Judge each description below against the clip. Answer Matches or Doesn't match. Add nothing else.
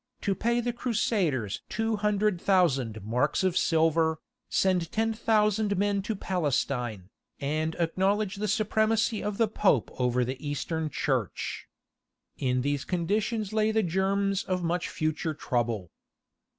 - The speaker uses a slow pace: Matches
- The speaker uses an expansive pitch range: Matches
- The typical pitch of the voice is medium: Matches